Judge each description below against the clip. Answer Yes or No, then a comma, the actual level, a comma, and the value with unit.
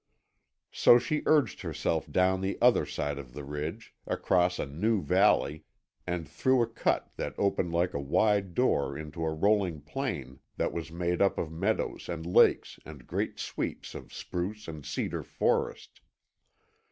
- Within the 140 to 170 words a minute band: Yes, average, 160 wpm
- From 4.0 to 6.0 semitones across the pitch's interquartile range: Yes, average, 5.0 semitones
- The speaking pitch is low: Yes, very low, 90 Hz